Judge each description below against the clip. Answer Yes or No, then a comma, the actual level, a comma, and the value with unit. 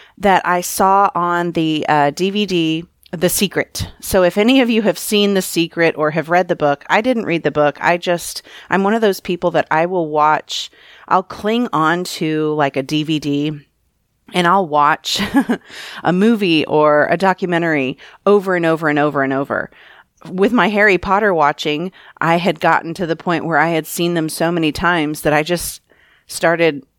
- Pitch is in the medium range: Yes, medium, 170 Hz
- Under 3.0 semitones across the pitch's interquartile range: No, average, 3.5 semitones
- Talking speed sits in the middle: Yes, average, 185 wpm